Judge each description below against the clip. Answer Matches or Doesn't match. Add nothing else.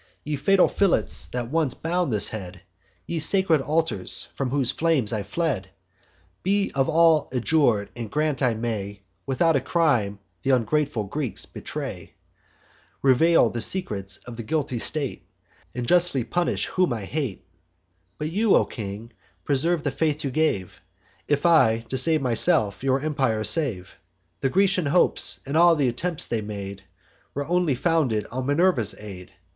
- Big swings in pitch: Matches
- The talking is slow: Doesn't match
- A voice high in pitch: Doesn't match